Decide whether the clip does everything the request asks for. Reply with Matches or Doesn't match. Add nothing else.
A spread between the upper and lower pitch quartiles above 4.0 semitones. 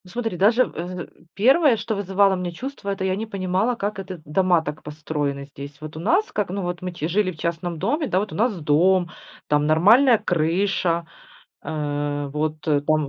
Matches